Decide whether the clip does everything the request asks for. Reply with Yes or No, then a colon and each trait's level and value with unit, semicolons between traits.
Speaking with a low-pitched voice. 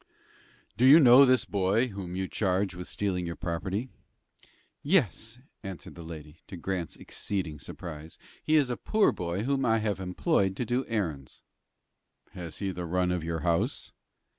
Yes: very low, 95 Hz